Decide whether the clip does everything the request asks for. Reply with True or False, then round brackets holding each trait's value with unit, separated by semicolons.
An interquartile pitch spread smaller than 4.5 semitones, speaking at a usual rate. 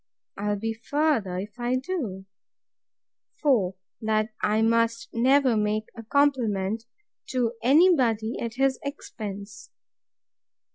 False (3.7 semitones; 110 wpm)